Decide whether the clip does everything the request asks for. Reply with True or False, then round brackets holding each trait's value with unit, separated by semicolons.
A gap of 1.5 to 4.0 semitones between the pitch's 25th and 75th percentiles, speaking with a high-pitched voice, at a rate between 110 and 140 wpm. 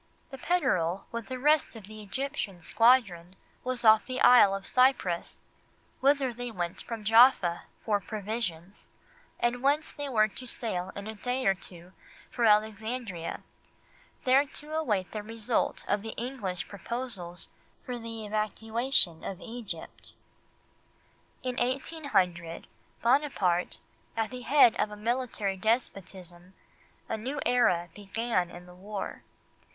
False (4.7 semitones; 220 Hz; 135 wpm)